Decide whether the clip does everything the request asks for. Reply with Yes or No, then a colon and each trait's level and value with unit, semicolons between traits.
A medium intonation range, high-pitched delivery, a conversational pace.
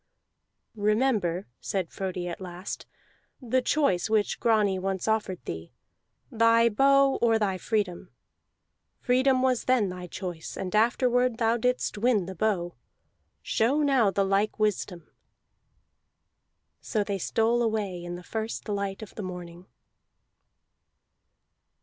No: average, 4.1 semitones; high, 210 Hz; slow, 125 wpm